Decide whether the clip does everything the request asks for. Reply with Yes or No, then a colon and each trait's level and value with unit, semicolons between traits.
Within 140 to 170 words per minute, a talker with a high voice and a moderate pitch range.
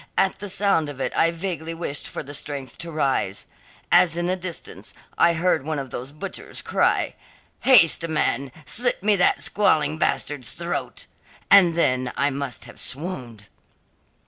No: average, 160 wpm; medium, 160 Hz; average, 4.5 semitones